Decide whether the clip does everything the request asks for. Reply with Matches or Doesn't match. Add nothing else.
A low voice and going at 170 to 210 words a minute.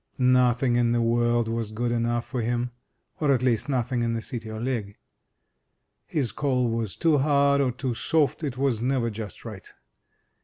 Matches